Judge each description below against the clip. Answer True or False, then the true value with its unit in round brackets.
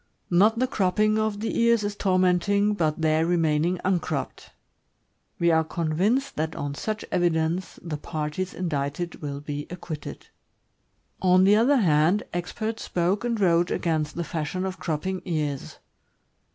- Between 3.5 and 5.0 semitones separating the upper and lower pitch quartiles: True (4.3 semitones)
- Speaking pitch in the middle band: True (175 Hz)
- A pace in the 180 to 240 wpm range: False (140 wpm)